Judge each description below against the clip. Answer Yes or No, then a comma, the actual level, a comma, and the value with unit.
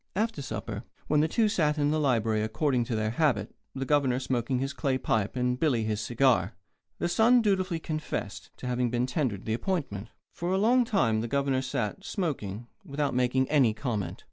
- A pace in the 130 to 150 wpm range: No, average, 190 wpm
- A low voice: Yes, low, 130 Hz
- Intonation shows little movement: No, average, 5.1 semitones